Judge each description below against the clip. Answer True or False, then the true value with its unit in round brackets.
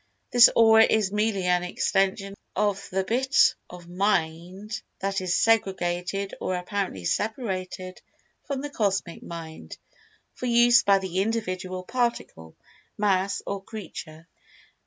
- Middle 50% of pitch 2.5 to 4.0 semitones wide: True (3.4 semitones)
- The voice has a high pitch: True (195 Hz)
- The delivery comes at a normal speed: False (120 wpm)